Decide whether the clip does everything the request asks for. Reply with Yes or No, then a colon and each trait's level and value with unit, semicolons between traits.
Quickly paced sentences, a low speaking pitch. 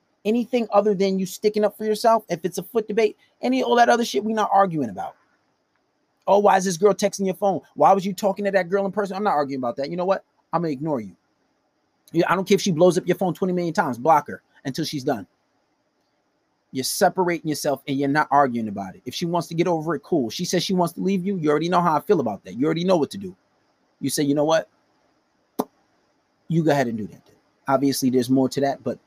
No: fast, 255 wpm; medium, 180 Hz